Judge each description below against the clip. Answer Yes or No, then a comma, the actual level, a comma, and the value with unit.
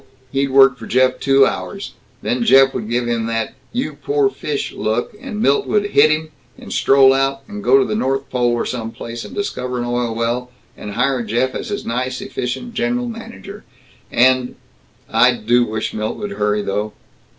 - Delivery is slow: No, average, 190 wpm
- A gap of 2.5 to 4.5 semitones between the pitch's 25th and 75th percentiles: No, average, 4.9 semitones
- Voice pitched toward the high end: No, low, 130 Hz